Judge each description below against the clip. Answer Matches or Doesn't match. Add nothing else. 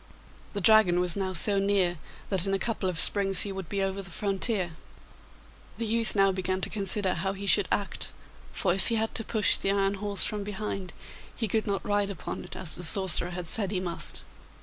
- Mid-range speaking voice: Doesn't match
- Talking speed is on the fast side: Matches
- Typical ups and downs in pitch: Doesn't match